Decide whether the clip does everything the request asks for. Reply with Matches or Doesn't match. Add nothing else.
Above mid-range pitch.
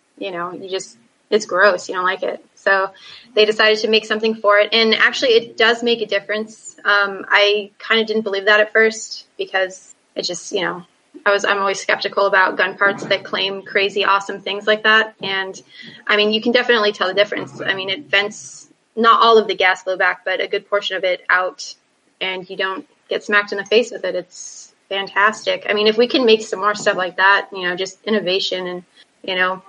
Matches